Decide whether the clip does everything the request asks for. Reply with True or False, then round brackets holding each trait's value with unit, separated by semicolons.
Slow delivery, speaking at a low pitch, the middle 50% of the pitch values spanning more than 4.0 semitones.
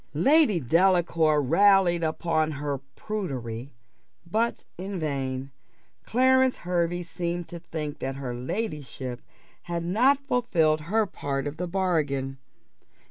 False (120 wpm; 170 Hz; 5.2 semitones)